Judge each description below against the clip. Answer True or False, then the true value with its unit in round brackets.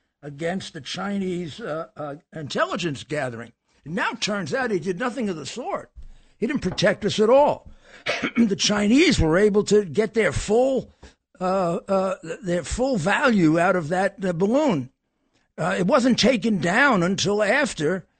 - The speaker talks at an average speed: True (165 wpm)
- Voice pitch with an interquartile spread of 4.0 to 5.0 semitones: True (4.7 semitones)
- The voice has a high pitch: True (195 Hz)